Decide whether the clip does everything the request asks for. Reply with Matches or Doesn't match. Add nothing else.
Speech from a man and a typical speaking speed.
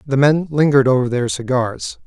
Matches